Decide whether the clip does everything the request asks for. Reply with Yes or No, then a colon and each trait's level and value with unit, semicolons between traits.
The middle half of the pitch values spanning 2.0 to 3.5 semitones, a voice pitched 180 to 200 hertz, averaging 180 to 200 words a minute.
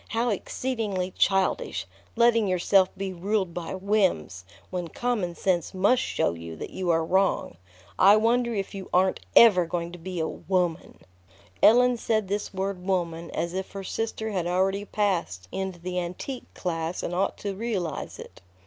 No: average, 3.0 semitones; high, 190 Hz; average, 165 wpm